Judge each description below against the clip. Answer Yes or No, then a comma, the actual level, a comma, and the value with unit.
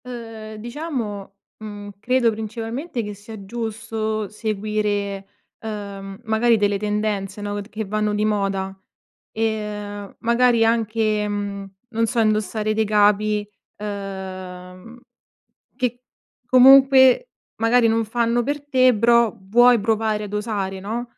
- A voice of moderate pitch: No, high, 215 Hz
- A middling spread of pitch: No, narrow, 2.3 semitones